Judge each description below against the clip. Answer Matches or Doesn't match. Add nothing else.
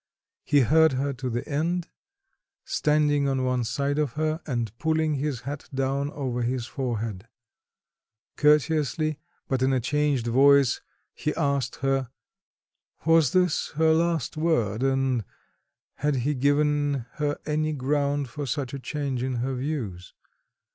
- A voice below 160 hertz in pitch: Matches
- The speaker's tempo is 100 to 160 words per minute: Matches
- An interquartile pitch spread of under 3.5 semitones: Matches